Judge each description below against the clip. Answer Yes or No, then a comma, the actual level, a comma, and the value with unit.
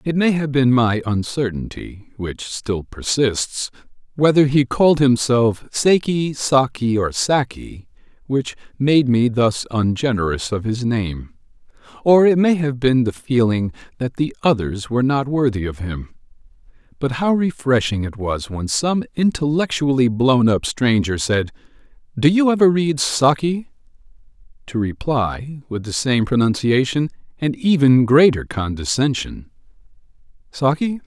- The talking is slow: Yes, slow, 130 wpm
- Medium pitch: No, low, 130 Hz